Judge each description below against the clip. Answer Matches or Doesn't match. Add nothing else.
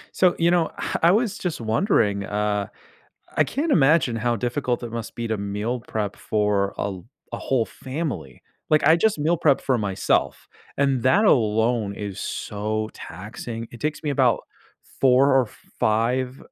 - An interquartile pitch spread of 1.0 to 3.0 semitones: Doesn't match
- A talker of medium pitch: Doesn't match